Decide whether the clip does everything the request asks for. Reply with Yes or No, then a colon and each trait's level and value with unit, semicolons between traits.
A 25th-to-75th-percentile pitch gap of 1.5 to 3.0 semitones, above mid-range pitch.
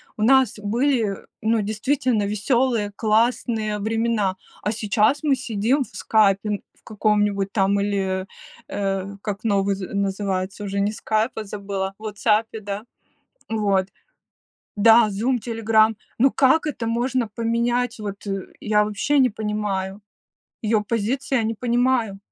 Yes: narrow, 2.5 semitones; high, 215 Hz